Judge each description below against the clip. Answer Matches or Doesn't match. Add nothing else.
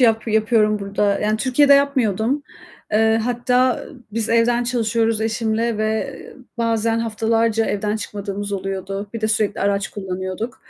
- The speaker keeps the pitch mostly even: Matches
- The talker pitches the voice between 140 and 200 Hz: Doesn't match